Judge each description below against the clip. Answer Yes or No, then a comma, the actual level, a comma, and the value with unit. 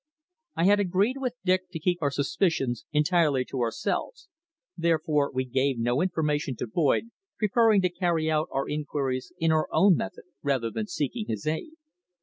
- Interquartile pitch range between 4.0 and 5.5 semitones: Yes, average, 5.1 semitones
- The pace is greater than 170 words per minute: No, average, 165 wpm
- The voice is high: No, medium, 155 Hz